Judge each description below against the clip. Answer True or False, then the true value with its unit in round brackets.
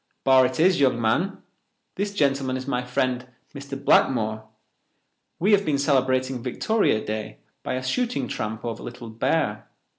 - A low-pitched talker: True (130 Hz)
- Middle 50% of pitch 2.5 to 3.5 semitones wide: True (3.0 semitones)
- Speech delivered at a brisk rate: False (150 wpm)